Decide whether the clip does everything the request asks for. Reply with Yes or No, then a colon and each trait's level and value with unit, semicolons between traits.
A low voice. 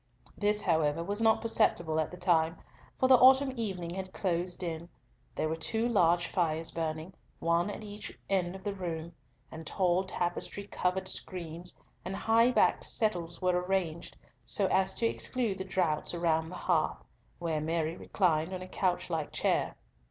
No: medium, 180 Hz